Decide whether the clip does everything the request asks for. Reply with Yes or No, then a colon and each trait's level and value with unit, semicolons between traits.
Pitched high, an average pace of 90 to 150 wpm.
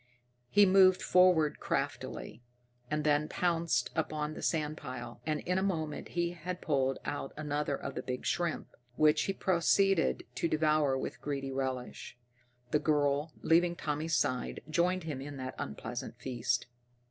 No: medium, 150 Hz; average, 145 wpm